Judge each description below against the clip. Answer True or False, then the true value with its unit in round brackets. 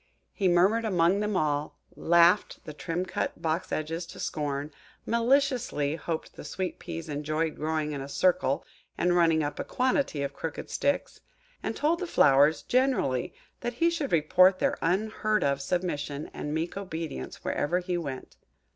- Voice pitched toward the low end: False (170 Hz)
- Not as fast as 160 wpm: True (150 wpm)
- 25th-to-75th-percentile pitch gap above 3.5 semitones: True (5.5 semitones)